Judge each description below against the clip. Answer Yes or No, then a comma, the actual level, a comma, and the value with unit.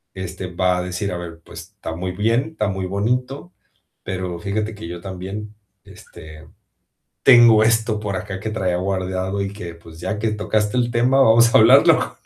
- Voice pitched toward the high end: No, low, 100 Hz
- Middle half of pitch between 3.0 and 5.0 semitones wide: Yes, average, 3.4 semitones